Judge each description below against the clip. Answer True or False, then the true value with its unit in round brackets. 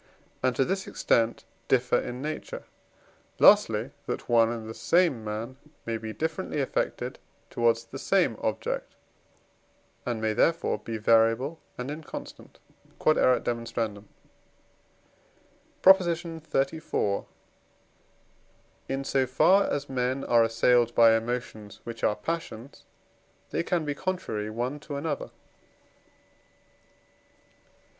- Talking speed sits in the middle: False (110 wpm)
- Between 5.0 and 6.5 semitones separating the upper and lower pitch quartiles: True (5.3 semitones)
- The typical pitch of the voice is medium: False (125 Hz)